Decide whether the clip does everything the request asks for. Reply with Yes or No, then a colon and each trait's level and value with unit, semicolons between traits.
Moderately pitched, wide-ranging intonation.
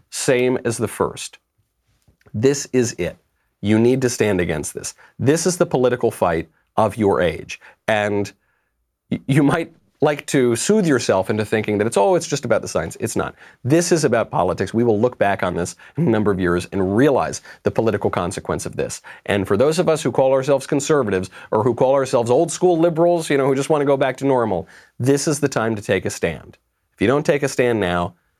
No: low, 125 Hz; wide, 5.7 semitones